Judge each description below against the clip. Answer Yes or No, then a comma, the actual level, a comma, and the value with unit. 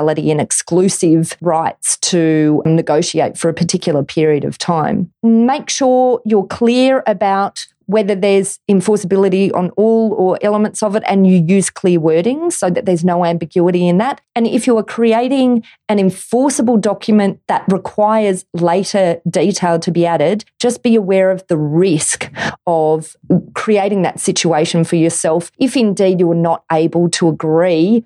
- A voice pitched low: No, high, 190 Hz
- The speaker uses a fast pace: No, average, 155 wpm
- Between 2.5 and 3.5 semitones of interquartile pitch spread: No, average, 4.1 semitones